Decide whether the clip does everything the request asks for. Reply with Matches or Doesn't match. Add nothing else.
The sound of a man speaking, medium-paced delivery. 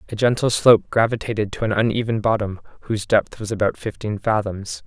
Matches